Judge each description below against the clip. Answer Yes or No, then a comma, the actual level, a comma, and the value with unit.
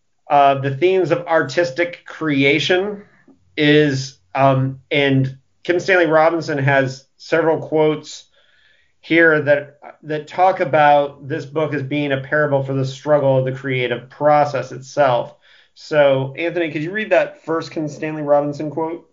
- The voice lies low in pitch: No, medium, 150 Hz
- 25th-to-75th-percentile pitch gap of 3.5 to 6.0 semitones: No, average, 2.9 semitones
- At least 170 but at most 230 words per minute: No, average, 140 wpm